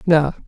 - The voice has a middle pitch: Yes, medium, 160 Hz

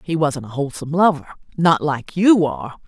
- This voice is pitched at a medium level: Yes, medium, 155 Hz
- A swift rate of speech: No, average, 165 wpm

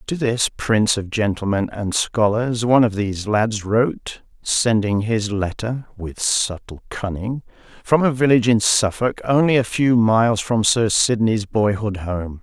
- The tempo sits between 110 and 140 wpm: No, average, 155 wpm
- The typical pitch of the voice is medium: No, low, 110 Hz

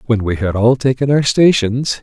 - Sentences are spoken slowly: No, fast, 205 wpm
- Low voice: Yes, low, 120 Hz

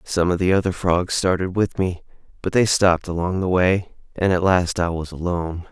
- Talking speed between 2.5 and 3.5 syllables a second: No, 5.2 syllables/s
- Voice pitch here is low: Yes, very low, 90 Hz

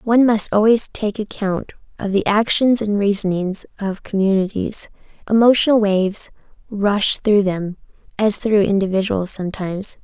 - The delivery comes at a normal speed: No, slow, 125 wpm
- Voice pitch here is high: Yes, high, 205 Hz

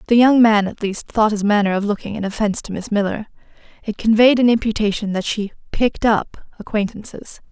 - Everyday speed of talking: Yes, average, 190 wpm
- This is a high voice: Yes, high, 215 Hz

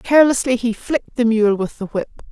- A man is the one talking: No, female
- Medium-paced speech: No, fast, 210 wpm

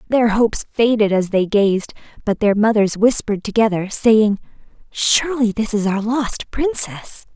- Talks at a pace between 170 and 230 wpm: No, average, 145 wpm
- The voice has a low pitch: No, high, 215 Hz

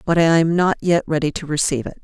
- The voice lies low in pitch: No, medium, 160 Hz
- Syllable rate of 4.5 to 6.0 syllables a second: No, 6.5 syllables/s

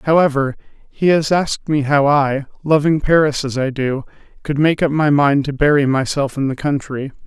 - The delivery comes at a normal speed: Yes, average, 190 wpm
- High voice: No, medium, 145 Hz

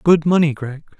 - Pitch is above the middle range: No, medium, 155 Hz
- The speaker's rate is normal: Yes, average, 180 wpm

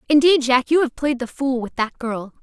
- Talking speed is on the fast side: Yes, fast, 250 wpm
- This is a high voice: Yes, very high, 265 Hz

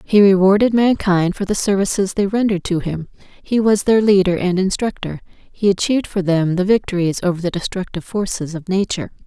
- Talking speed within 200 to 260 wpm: No, average, 180 wpm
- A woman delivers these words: Yes, female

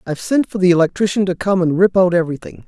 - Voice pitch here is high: No, medium, 180 Hz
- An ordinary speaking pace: No, fast, 245 wpm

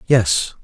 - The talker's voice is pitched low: Yes, low, 125 Hz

